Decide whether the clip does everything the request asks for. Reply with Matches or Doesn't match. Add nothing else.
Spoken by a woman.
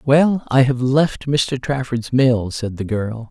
Doesn't match